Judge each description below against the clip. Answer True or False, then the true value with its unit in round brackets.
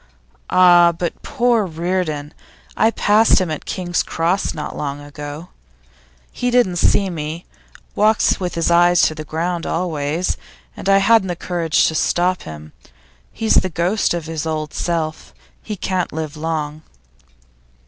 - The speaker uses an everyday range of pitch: True (3.0 semitones)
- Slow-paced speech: False (150 wpm)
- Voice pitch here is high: False (170 Hz)